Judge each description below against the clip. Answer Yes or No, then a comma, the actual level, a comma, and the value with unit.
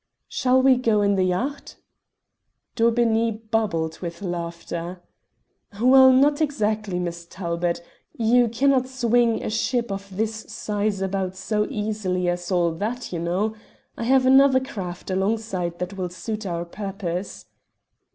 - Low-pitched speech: No, high, 210 Hz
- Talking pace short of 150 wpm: Yes, slow, 135 wpm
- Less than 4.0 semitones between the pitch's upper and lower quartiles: No, average, 4.7 semitones